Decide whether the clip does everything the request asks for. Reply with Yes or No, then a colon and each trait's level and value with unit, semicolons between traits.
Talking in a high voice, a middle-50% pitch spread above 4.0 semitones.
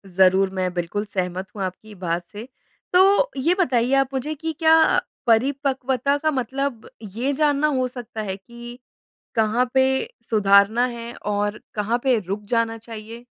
Yes: high, 235 Hz; average, 4.6 semitones